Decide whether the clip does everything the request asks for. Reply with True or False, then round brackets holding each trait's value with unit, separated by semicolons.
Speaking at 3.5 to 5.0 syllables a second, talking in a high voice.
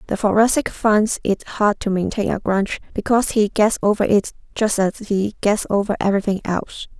False (5.4 syllables/s; 205 Hz)